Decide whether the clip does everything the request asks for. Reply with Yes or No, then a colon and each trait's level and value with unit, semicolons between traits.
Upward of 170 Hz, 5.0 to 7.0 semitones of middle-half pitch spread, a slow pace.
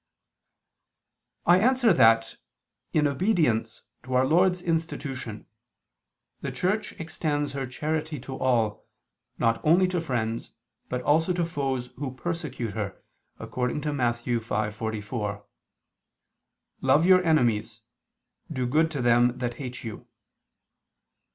No: low, 130 Hz; wide, 5.5 semitones; slow, 115 wpm